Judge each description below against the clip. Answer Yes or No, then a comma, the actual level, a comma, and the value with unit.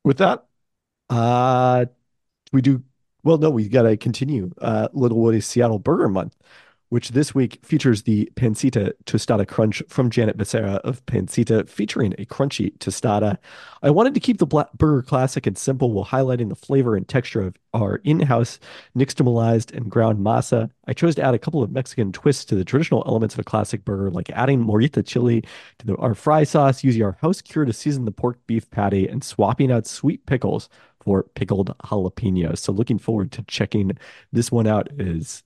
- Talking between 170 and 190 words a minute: Yes, average, 185 wpm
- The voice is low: Yes, low, 120 Hz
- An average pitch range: Yes, average, 3.9 semitones